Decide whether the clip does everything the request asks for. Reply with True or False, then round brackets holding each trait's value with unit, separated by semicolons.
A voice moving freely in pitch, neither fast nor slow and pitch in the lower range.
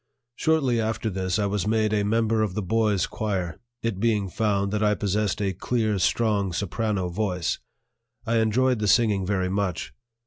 False (2.5 semitones; 170 wpm; 105 Hz)